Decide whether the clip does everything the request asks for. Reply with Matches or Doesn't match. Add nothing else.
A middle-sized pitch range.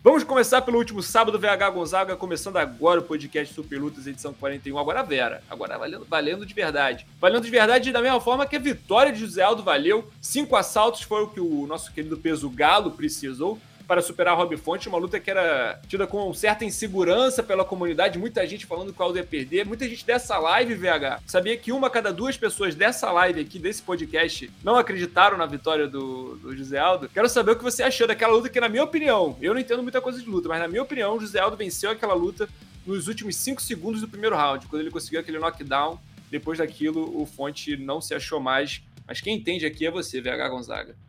Doesn't match